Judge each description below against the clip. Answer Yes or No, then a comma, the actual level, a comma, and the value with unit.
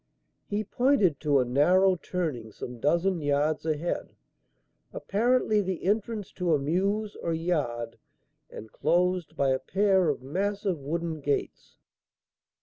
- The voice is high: No, medium, 170 Hz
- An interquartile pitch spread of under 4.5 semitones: No, average, 5.1 semitones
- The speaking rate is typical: No, slow, 130 wpm